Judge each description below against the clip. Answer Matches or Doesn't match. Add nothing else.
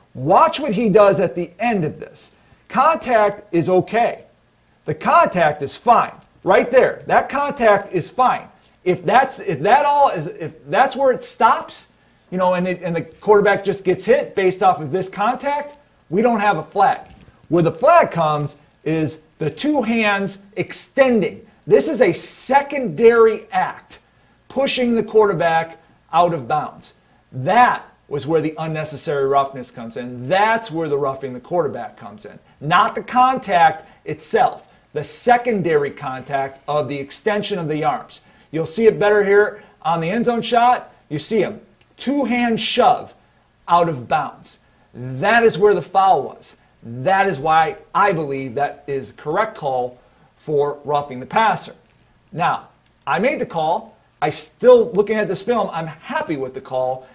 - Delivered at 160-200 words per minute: Matches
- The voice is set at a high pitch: Matches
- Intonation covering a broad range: Matches